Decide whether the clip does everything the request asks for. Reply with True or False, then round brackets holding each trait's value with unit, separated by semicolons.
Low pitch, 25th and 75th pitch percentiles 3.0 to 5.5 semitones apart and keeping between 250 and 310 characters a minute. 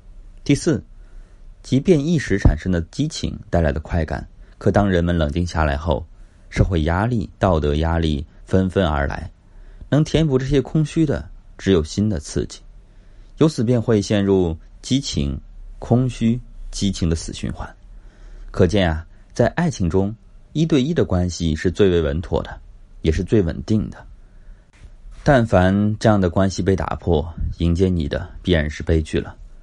False (95 Hz; 4.1 semitones; 225 characters per minute)